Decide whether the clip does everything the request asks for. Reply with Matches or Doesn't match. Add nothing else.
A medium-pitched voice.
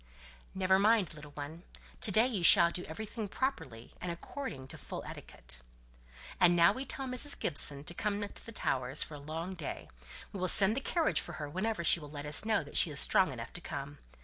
Matches